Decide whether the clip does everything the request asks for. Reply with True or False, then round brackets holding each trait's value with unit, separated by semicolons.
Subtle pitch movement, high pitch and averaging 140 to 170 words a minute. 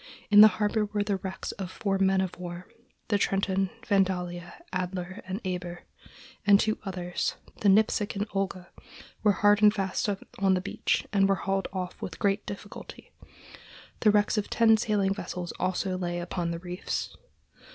True (2.1 semitones; 195 Hz; 165 wpm)